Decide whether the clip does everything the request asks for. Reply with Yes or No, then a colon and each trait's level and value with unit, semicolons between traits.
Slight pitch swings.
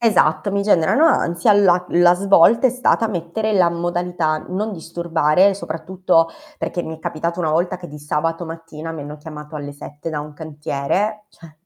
No: average, 3.3 semitones